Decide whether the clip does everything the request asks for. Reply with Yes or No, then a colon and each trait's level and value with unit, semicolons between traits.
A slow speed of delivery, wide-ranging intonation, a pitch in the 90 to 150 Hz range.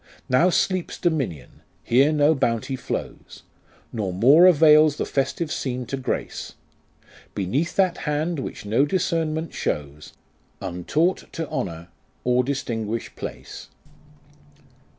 Yes: slow, 110 wpm; wide, 5.7 semitones; medium, 140 Hz